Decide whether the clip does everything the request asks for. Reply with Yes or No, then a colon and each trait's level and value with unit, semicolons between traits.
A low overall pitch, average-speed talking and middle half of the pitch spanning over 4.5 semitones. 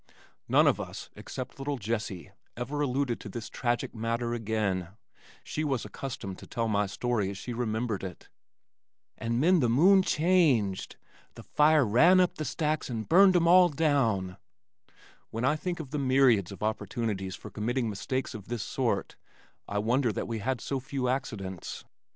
Yes: low, 120 Hz; average, 170 wpm; average, 4.9 semitones